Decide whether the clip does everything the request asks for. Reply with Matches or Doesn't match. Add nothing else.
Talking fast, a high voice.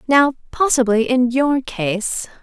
Doesn't match